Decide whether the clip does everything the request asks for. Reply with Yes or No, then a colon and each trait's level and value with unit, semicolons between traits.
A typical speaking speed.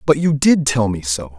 No: fast, 260 wpm